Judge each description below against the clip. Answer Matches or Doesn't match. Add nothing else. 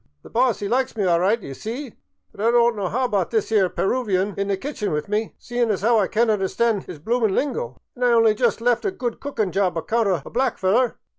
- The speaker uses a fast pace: Matches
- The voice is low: Doesn't match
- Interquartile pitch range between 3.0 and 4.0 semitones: Matches